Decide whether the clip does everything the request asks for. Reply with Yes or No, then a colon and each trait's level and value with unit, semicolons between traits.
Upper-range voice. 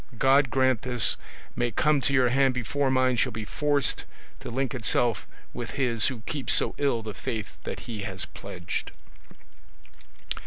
No: low, 125 Hz